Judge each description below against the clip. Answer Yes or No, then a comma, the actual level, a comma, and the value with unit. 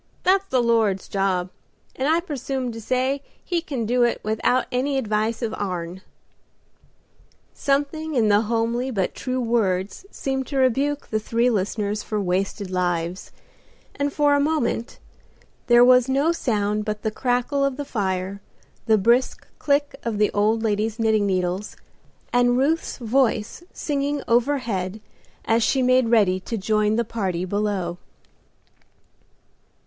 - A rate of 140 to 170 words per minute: Yes, average, 145 wpm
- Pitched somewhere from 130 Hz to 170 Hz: No, high, 230 Hz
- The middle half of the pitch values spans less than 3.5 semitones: No, average, 4.4 semitones